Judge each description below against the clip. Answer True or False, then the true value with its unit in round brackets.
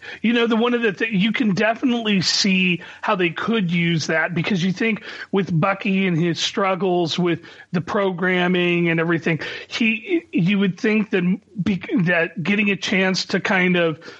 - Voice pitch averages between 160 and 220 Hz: True (190 Hz)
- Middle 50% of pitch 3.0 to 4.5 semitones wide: True (3.4 semitones)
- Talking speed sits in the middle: True (175 wpm)